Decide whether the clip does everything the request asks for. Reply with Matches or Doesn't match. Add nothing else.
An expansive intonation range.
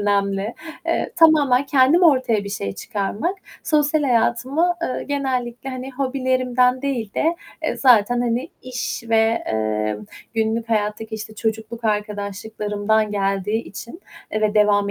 Doesn't match